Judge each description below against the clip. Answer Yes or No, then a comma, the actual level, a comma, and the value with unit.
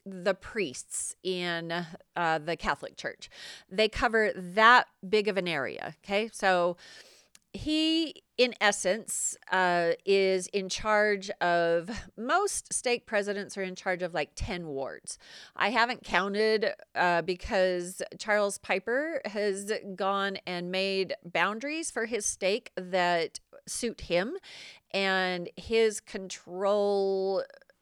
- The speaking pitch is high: Yes, high, 195 Hz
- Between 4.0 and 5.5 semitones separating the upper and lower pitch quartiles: No, average, 3.1 semitones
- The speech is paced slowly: Yes, slow, 115 wpm